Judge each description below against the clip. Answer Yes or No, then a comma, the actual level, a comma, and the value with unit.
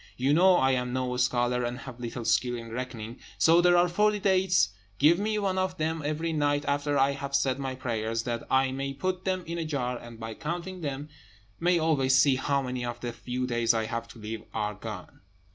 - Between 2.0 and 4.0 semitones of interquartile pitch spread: No, average, 5.1 semitones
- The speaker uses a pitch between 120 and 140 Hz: Yes, low, 135 Hz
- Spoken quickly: Yes, fast, 220 wpm